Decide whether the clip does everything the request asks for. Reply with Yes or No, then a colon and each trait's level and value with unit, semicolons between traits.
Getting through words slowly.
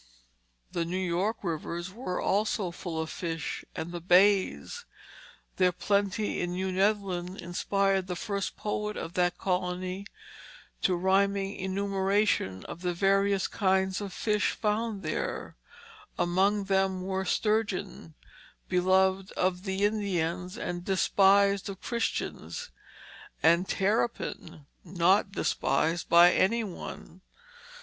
Yes: slow, 115 wpm